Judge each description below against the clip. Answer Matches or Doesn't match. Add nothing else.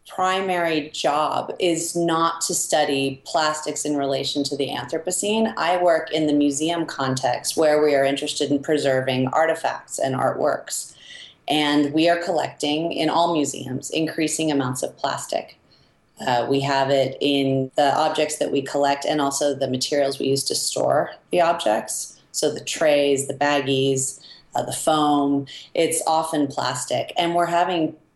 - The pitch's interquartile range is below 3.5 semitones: Matches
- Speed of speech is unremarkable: Matches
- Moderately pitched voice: Matches